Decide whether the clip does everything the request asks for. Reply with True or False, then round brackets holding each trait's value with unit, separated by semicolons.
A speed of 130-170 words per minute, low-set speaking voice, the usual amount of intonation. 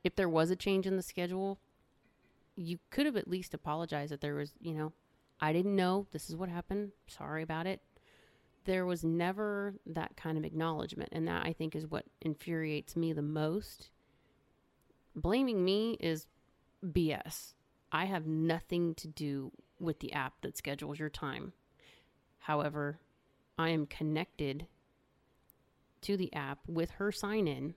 False (160 wpm; 165 Hz; 3.4 semitones)